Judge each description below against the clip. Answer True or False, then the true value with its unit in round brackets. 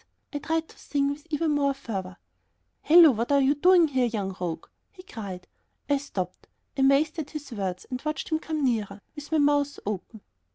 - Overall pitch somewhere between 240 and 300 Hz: True (280 Hz)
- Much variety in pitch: True (6.0 semitones)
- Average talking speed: True (190 wpm)